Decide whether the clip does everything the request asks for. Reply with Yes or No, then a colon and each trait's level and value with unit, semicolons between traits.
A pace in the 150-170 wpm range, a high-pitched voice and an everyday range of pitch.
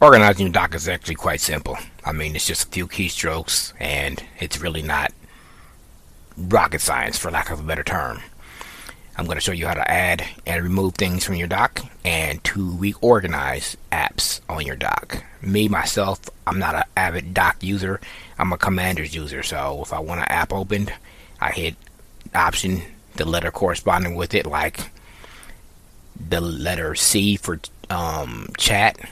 No: average, 165 wpm; very low, 90 Hz; average, 3.2 semitones